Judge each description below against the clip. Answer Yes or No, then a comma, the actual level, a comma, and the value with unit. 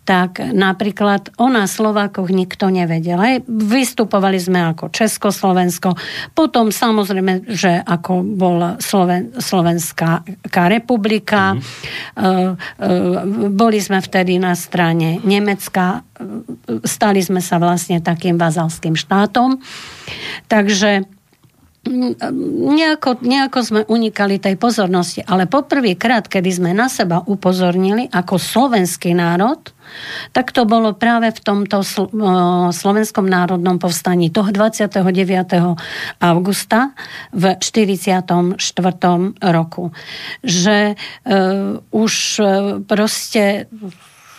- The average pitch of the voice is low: No, high, 195 Hz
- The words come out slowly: Yes, slow, 90 wpm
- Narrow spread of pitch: No, average, 3.4 semitones